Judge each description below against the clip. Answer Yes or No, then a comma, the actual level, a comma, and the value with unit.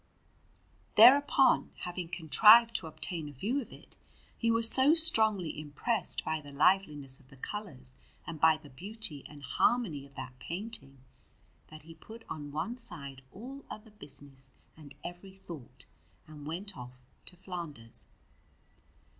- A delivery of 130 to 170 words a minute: Yes, average, 145 wpm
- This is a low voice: No, medium, 165 Hz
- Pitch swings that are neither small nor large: No, wide, 7.3 semitones